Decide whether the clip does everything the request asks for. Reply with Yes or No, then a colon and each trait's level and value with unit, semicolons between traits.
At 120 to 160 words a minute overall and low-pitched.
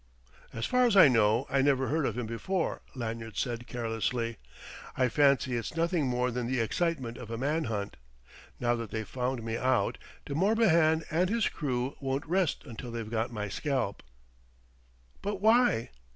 No: average, 170 wpm; low, 130 Hz